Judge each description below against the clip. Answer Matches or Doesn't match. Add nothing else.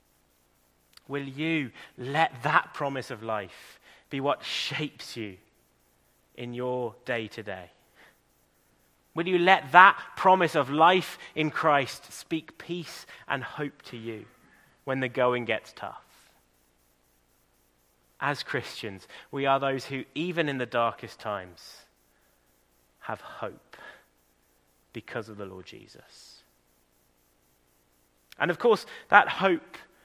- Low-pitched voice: Matches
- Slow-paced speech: Matches